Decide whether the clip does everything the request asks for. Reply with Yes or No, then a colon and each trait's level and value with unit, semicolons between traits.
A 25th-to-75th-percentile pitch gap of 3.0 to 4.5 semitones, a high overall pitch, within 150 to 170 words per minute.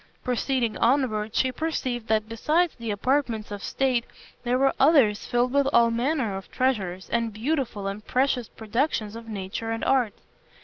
Yes: average, 3.6 semitones; high, 235 Hz; average, 160 wpm